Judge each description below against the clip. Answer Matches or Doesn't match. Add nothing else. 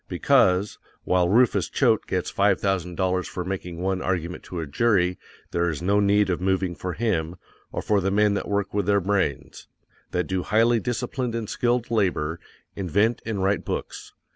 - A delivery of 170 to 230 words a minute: Matches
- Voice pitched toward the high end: Doesn't match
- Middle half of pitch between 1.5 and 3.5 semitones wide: Matches